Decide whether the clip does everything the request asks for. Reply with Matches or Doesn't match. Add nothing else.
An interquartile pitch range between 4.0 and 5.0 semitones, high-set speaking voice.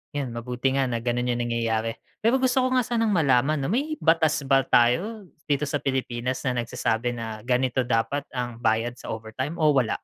Doesn't match